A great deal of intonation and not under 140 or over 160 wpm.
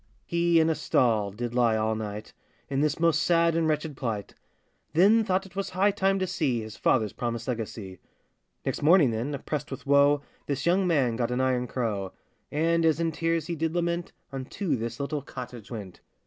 No: wide, 6.2 semitones; average, 190 wpm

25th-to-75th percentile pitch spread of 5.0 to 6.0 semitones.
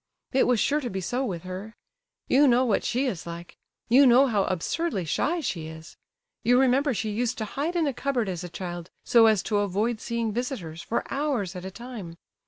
Yes: wide, 5.6 semitones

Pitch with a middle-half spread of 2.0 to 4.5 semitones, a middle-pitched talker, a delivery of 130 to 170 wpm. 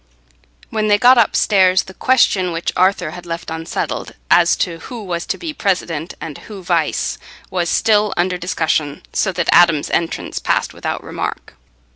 Yes: average, 3.6 semitones; medium, 180 Hz; average, 160 wpm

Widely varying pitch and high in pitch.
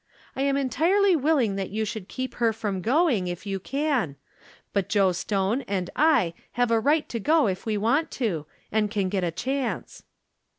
Yes: wide, 6.1 semitones; high, 225 Hz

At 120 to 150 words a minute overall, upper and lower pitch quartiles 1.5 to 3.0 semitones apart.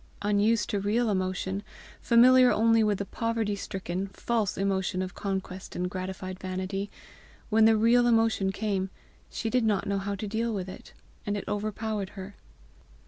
No: average, 160 wpm; average, 2.7 semitones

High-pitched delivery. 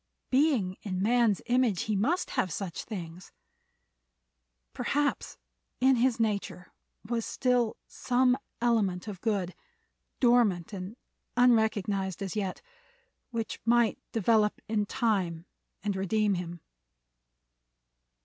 Yes: high, 215 Hz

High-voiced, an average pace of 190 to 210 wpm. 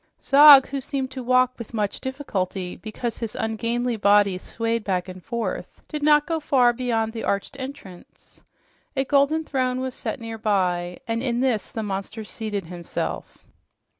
No: high, 230 Hz; average, 160 wpm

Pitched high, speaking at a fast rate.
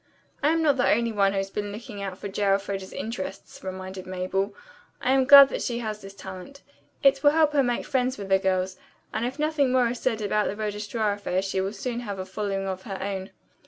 Yes: high, 205 Hz; fast, 235 wpm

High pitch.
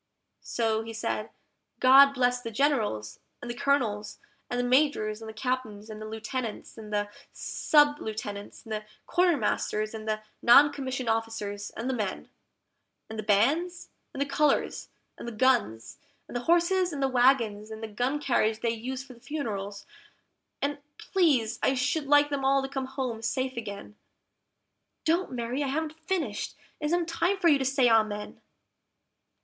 Yes: high, 245 Hz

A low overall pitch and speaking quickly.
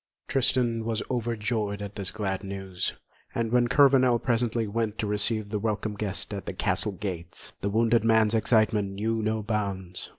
No: low, 110 Hz; average, 165 wpm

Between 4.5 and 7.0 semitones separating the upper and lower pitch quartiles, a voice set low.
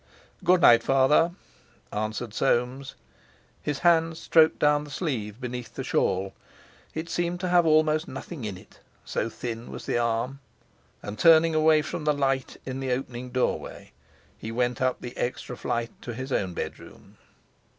Yes: average, 4.8 semitones; low, 130 Hz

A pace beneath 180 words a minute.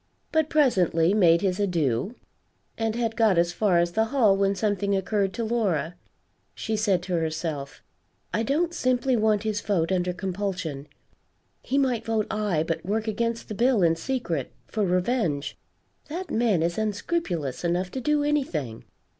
Yes: average, 160 wpm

